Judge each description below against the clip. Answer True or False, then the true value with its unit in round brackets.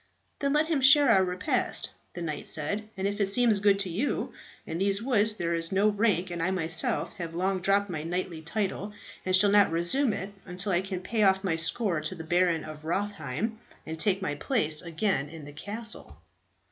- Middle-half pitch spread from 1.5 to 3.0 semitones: False (3.9 semitones)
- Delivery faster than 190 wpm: True (200 wpm)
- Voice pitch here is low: False (190 Hz)